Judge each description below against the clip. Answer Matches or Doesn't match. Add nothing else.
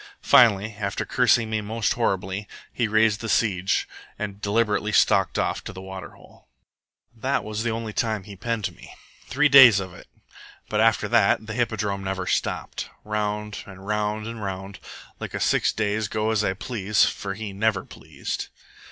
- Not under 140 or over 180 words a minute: Matches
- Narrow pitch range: Matches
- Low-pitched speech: Matches